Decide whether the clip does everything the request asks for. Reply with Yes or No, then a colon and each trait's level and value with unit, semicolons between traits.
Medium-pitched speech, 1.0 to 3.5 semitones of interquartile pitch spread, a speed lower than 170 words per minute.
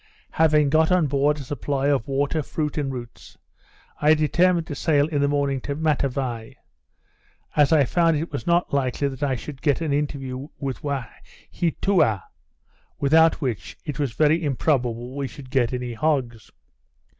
Yes: medium, 145 Hz; average, 2.8 semitones; average, 160 wpm